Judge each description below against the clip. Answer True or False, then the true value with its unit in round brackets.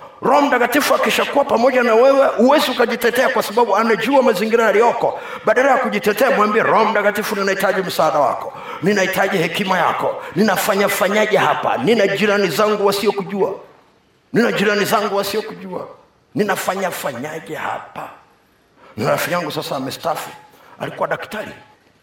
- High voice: True (215 Hz)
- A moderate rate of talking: True (110 wpm)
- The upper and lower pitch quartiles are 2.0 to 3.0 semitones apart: False (3.7 semitones)